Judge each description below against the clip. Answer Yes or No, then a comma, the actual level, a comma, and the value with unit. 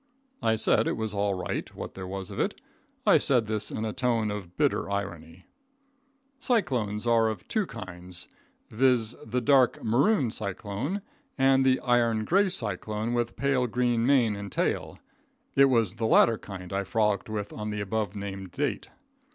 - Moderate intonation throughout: Yes, average, 3.7 semitones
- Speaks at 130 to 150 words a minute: No, average, 165 wpm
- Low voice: Yes, low, 110 Hz